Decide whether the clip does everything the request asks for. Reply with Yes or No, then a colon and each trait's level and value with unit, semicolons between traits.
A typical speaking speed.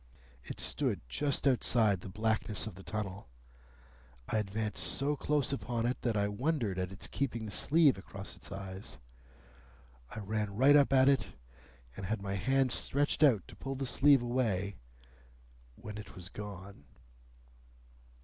Yes: average, 155 wpm